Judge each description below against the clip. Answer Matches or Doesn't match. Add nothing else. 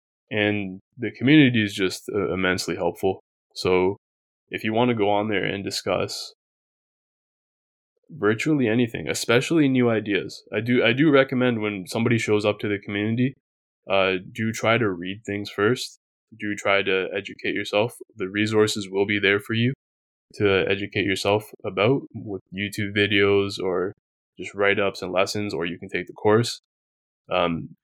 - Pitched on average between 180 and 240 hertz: Doesn't match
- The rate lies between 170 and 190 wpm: Doesn't match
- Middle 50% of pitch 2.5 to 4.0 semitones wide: Matches